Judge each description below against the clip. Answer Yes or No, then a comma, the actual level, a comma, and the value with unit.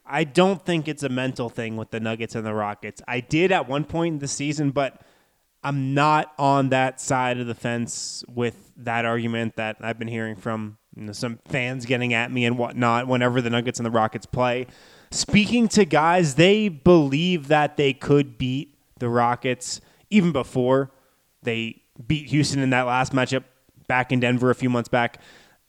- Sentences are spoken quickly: No, average, 190 wpm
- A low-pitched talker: Yes, low, 130 Hz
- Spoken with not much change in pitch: No, average, 3.4 semitones